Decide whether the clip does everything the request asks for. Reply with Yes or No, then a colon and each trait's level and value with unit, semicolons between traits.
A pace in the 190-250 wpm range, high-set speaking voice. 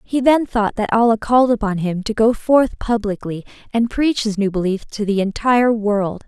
Yes: average, 200 wpm; high, 220 Hz